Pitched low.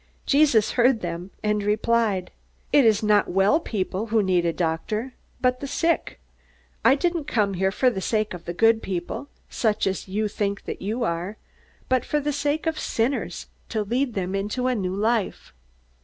No: high, 215 Hz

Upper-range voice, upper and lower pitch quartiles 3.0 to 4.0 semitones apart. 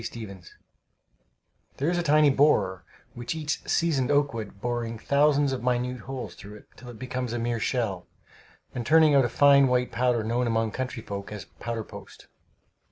No: low, 125 Hz; average, 3.7 semitones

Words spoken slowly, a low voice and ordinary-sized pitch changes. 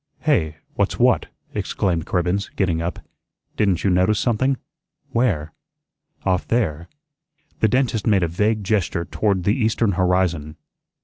Yes: slow, 130 wpm; very low, 95 Hz; average, 4.2 semitones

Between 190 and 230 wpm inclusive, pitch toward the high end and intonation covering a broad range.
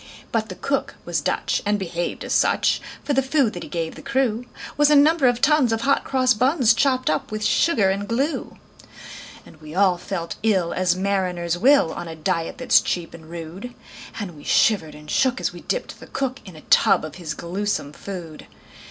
Yes: fast, 205 wpm; high, 205 Hz; wide, 7.1 semitones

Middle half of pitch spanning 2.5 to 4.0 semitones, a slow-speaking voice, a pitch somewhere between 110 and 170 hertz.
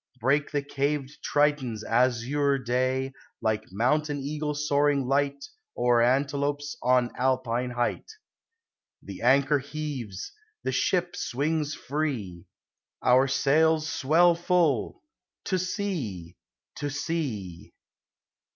Yes: average, 3.2 semitones; slow, 100 wpm; medium, 140 Hz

